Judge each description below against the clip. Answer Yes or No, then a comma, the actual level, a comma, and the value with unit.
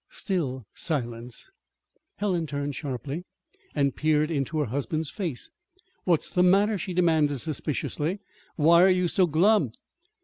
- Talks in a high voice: No, medium, 155 Hz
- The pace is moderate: No, slow, 130 wpm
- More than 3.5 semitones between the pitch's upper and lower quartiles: Yes, average, 4.1 semitones